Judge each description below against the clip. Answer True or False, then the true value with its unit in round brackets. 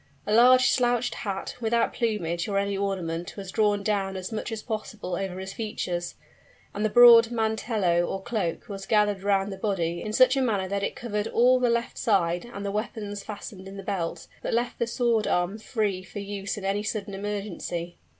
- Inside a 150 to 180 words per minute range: False (200 wpm)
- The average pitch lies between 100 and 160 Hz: False (205 Hz)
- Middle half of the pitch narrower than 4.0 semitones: True (2.6 semitones)